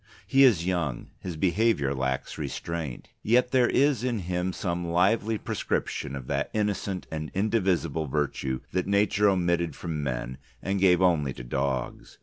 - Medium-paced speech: Yes, average, 150 wpm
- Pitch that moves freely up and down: Yes, wide, 6.1 semitones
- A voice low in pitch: Yes, very low, 90 Hz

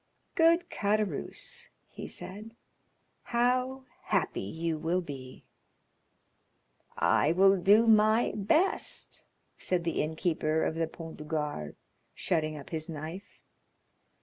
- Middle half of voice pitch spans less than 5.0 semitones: No, wide, 5.6 semitones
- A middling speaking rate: No, slow, 110 wpm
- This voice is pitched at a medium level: Yes, medium, 180 Hz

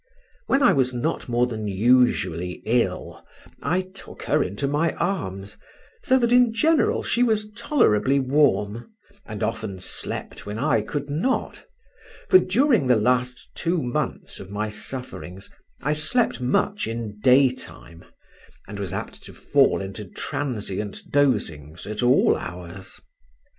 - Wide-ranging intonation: Yes, wide, 7.5 semitones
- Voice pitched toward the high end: No, low, 125 Hz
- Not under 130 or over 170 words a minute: Yes, slow, 135 wpm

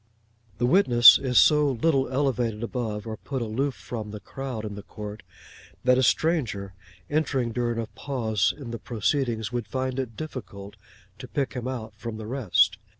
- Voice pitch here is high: No, low, 120 Hz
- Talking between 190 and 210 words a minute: No, average, 170 wpm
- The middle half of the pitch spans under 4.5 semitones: Yes, average, 3.5 semitones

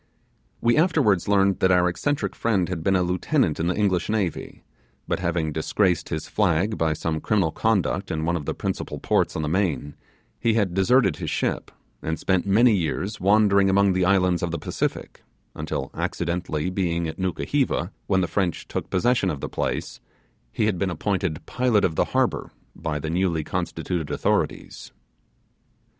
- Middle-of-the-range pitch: No, very low, 90 Hz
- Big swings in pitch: No, average, 3.3 semitones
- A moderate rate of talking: Yes, average, 175 wpm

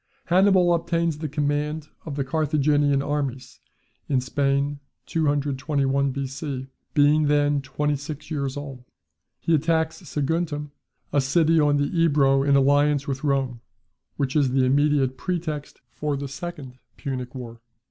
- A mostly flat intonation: Yes, narrow, 2.0 semitones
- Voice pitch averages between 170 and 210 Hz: No, medium, 145 Hz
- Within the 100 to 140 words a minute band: Yes, slow, 135 wpm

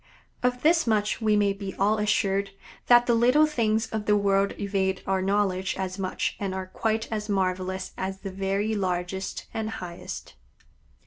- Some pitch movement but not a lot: No, narrow, 2.3 semitones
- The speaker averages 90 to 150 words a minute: No, average, 170 wpm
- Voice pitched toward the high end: Yes, high, 200 Hz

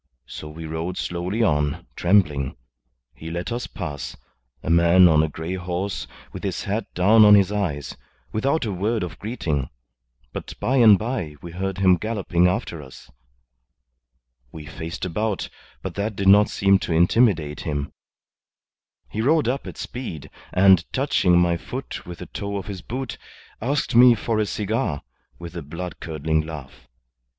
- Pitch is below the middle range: Yes, very low, 90 Hz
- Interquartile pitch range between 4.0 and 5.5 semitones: Yes, average, 4.8 semitones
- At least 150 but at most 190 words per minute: Yes, average, 160 wpm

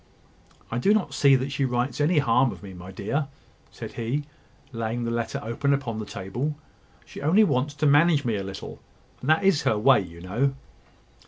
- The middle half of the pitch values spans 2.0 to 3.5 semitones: No, average, 4.5 semitones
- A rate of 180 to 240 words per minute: Yes, average, 195 wpm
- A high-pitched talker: No, low, 130 Hz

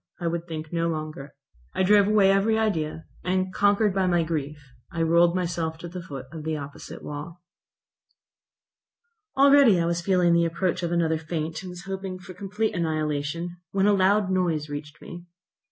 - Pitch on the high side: No, medium, 170 Hz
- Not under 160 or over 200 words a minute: Yes, average, 175 wpm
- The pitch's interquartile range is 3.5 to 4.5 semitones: No, average, 3.0 semitones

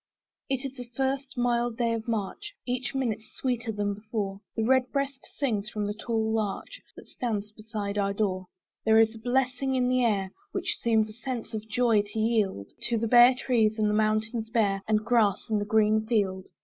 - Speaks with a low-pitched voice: No, high, 225 Hz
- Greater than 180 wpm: Yes, average, 195 wpm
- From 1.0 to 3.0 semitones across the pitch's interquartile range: Yes, average, 2.7 semitones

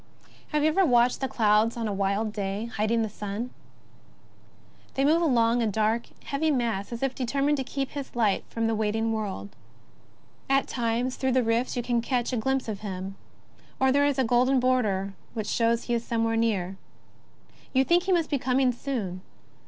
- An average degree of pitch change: Yes, average, 3.5 semitones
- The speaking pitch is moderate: No, high, 235 Hz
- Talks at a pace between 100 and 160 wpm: No, average, 190 wpm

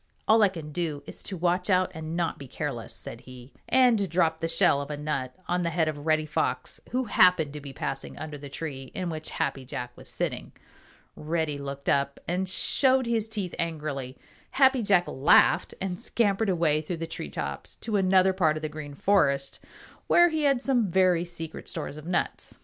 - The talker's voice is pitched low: No, medium, 165 Hz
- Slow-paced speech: No, average, 200 wpm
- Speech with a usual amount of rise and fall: Yes, average, 4.5 semitones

